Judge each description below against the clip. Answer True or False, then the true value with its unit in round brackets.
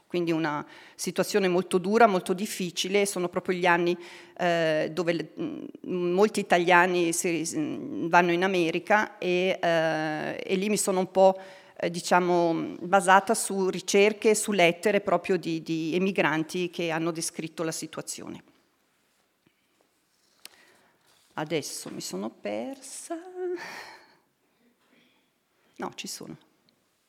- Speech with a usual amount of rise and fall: True (3.0 semitones)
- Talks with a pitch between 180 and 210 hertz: True (185 Hz)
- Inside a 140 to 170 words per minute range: False (115 wpm)